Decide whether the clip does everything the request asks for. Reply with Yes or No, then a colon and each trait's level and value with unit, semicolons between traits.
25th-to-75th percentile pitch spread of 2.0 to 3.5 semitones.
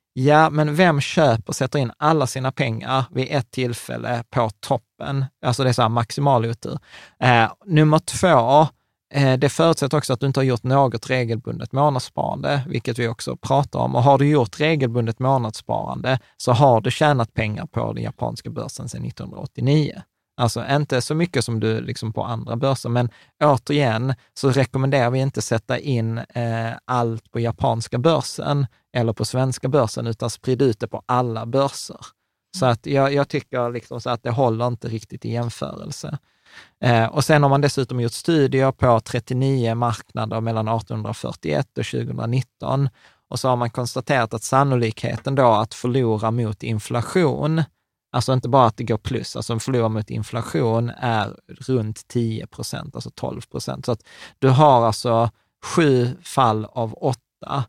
Yes: average, 3.1 semitones